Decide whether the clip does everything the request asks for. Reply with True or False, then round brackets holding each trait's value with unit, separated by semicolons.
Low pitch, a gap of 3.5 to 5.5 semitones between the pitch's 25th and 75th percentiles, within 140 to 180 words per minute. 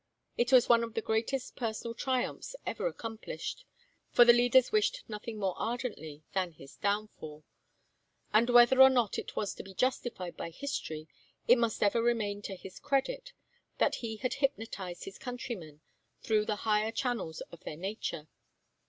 False (225 Hz; 4.2 semitones; 160 wpm)